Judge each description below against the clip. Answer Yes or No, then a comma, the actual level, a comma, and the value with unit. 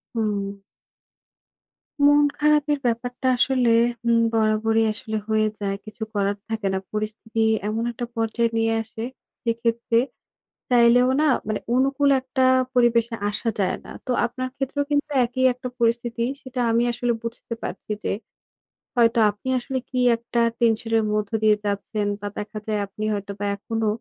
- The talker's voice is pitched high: Yes, high, 230 Hz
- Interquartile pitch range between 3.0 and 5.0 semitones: No, narrow, 2.4 semitones